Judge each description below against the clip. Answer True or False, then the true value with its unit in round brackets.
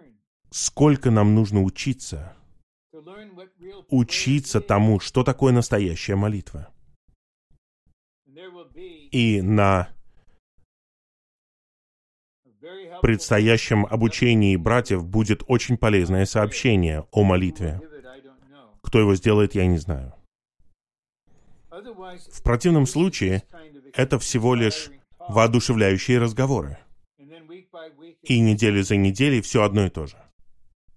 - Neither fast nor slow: False (85 wpm)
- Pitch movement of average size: False (6.2 semitones)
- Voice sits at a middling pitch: False (110 Hz)